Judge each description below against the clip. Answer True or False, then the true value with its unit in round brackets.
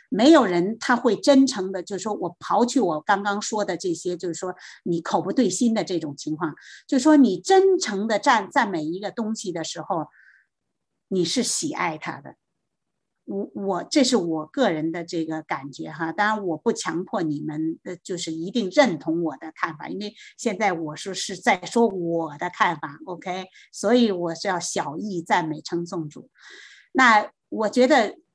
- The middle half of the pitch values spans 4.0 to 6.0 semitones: True (5.5 semitones)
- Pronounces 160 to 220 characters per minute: False (255 characters per minute)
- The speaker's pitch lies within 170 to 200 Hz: True (185 Hz)